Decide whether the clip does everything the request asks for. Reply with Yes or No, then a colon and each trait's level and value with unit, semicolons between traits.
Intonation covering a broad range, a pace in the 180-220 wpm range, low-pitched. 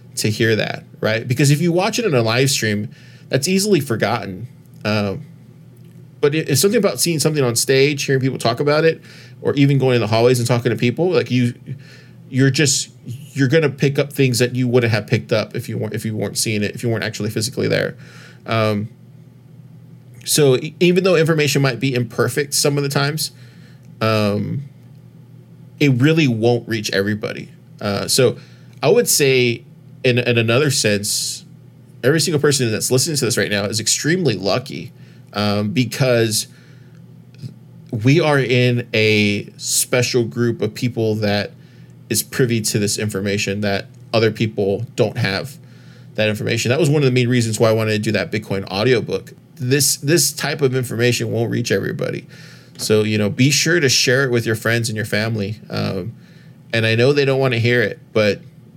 No: average, 4.2 semitones; average, 185 wpm; low, 125 Hz